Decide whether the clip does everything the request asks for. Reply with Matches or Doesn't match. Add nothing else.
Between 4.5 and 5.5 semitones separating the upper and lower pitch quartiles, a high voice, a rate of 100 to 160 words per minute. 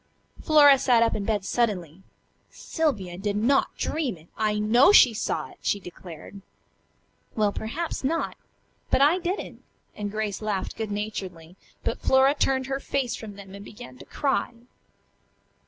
Matches